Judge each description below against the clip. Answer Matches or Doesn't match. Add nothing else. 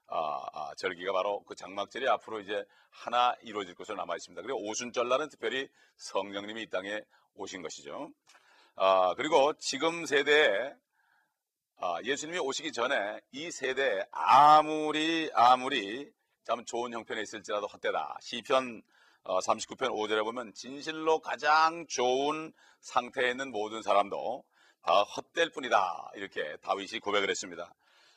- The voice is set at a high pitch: Doesn't match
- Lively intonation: Matches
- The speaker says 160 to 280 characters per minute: Doesn't match